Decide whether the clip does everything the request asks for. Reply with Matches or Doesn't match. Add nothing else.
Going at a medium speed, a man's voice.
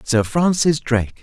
Matches